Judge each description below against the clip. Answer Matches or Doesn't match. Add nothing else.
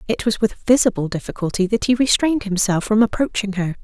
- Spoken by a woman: Matches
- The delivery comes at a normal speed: Matches